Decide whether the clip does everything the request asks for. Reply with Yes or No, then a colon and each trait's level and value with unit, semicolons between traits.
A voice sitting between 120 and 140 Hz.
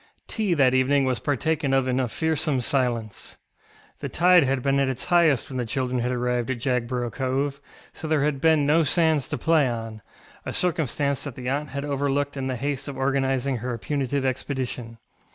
Yes: low, 135 Hz